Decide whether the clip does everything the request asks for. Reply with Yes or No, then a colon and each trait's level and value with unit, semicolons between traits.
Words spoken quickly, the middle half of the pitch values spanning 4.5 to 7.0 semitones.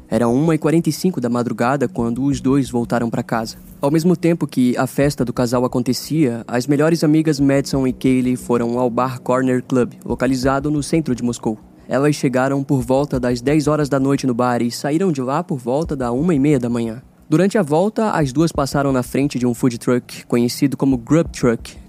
No: fast, 195 wpm; average, 3.3 semitones